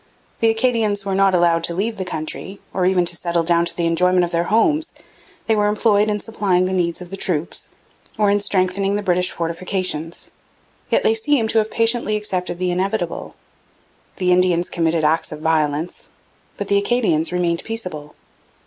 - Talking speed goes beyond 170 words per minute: Yes, average, 180 wpm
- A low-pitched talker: No, medium, 185 Hz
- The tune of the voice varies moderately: Yes, average, 3.5 semitones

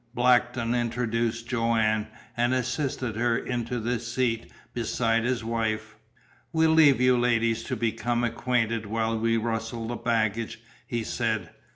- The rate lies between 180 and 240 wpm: No, slow, 135 wpm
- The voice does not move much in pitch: Yes, narrow, 1.4 semitones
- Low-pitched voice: Yes, low, 115 Hz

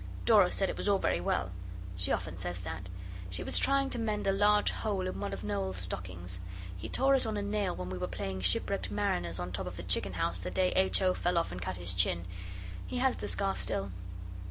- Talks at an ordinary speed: No, fast, 235 wpm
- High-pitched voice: No, very low, 95 Hz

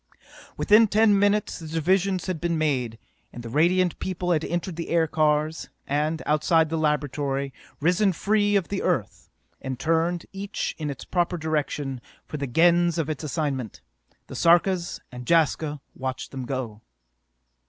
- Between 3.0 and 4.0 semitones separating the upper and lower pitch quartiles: Yes, average, 3.5 semitones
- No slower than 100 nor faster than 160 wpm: Yes, average, 155 wpm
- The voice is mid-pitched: Yes, medium, 160 Hz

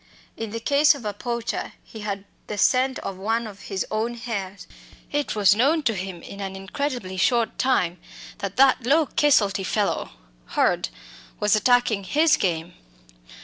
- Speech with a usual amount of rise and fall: Yes, average, 4.5 semitones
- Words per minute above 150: Yes, average, 160 wpm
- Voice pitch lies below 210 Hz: No, high, 220 Hz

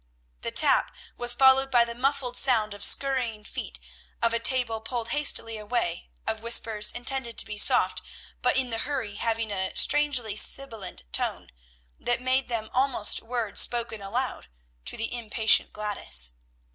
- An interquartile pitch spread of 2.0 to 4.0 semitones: Yes, average, 2.9 semitones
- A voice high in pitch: Yes, high, 235 Hz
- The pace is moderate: Yes, average, 155 wpm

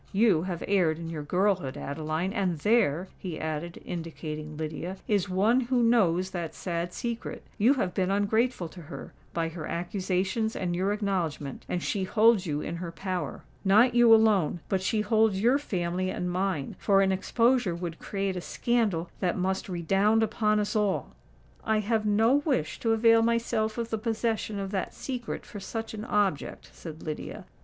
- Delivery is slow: No, average, 170 wpm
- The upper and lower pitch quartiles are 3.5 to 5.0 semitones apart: Yes, average, 4.2 semitones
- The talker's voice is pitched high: Yes, high, 195 Hz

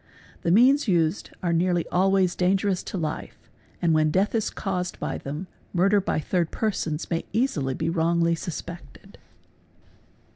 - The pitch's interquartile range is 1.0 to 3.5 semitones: Yes, average, 2.9 semitones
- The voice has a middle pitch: Yes, medium, 175 Hz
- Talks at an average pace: Yes, average, 145 wpm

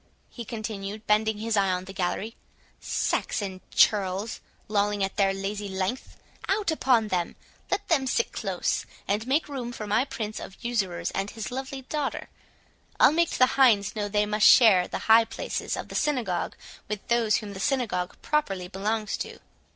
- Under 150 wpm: No, average, 165 wpm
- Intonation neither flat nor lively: Yes, average, 3.8 semitones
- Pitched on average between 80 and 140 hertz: No, high, 215 Hz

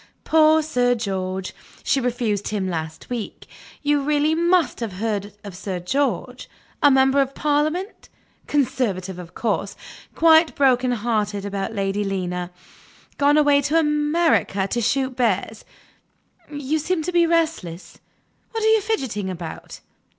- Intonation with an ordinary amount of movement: No, wide, 7.1 semitones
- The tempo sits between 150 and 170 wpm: No, slow, 135 wpm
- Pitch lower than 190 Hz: No, very high, 250 Hz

